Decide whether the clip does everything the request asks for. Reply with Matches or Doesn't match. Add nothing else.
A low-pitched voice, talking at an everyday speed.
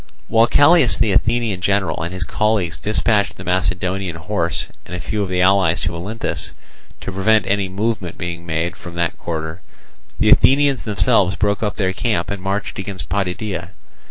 Matches